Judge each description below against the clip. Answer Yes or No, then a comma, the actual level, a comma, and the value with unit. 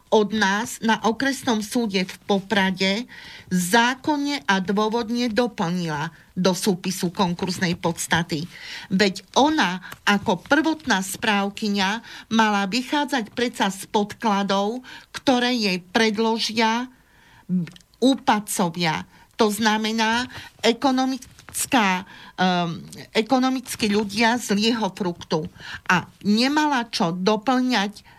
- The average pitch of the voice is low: No, high, 215 Hz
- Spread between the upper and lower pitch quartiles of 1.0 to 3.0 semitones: No, average, 4.0 semitones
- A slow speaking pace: Yes, slow, 85 wpm